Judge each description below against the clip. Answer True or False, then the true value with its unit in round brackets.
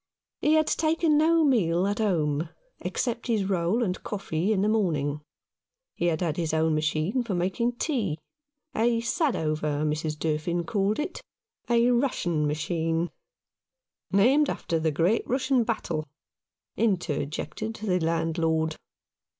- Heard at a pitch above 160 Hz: True (185 Hz)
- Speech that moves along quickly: False (135 wpm)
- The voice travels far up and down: True (6.8 semitones)